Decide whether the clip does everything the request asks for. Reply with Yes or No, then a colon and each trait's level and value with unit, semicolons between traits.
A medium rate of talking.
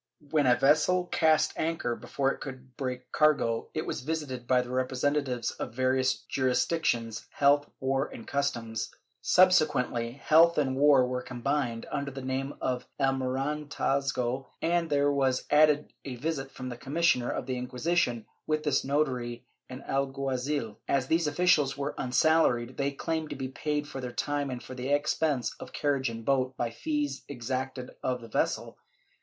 Yes: average, 165 wpm